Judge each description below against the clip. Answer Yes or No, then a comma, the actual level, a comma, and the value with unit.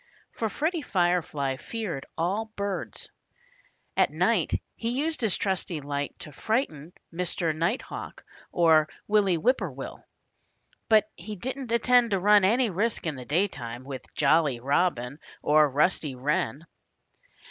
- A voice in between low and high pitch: Yes, medium, 175 Hz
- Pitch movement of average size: No, wide, 6.7 semitones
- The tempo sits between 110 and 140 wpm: Yes, slow, 135 wpm